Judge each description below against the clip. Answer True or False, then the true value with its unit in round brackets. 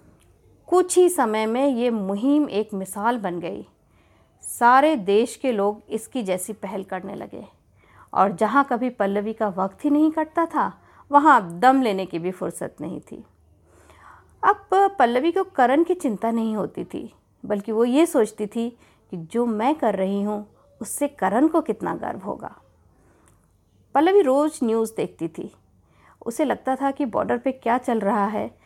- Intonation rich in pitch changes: True (5.9 semitones)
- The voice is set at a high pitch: True (230 Hz)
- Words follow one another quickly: False (165 wpm)